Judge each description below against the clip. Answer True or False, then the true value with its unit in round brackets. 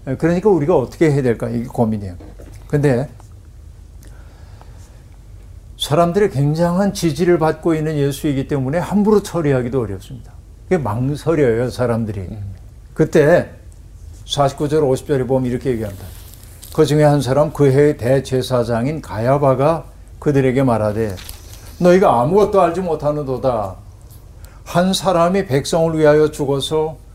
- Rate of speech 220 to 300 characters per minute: True (295 characters per minute)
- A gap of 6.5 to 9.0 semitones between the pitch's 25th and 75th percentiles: True (7.0 semitones)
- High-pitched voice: False (130 Hz)